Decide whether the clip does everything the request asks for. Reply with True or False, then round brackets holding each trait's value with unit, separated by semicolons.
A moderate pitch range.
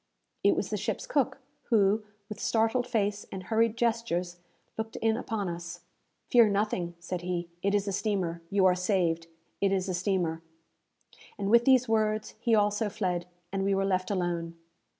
True (3.6 semitones)